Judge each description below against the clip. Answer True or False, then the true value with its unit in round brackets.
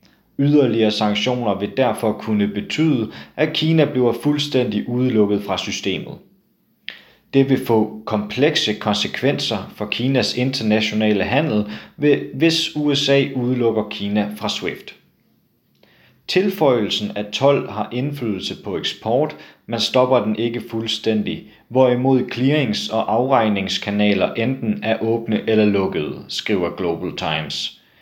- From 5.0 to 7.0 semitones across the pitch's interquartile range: False (4.0 semitones)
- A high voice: False (115 Hz)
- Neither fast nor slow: False (110 wpm)